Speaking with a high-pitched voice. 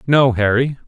No: low, 125 Hz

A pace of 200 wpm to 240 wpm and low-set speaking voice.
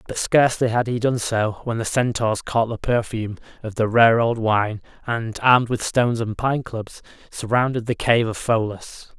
No: average, 190 wpm; low, 115 Hz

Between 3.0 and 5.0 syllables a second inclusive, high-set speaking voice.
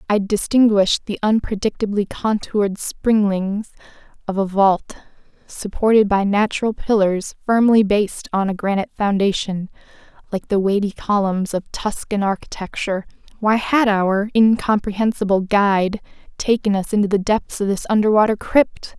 Yes: 4.9 syllables/s; high, 205 Hz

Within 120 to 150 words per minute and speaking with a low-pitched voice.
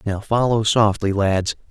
Yes: average, 140 wpm; low, 105 Hz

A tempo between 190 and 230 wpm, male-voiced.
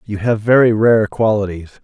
No: average, 165 wpm; male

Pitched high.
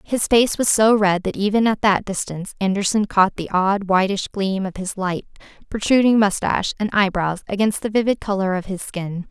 Yes: high, 200 Hz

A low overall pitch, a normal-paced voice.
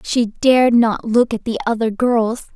No: high, 230 Hz; average, 190 wpm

